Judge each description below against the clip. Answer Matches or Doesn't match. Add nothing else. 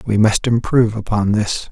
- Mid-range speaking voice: Doesn't match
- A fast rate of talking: Doesn't match